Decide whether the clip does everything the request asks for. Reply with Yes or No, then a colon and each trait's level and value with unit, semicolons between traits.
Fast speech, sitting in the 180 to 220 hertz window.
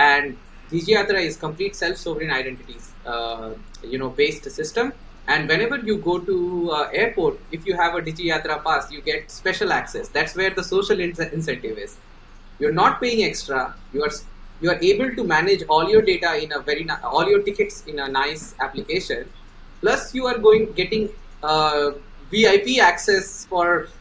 No: average, 175 wpm; medium, 185 Hz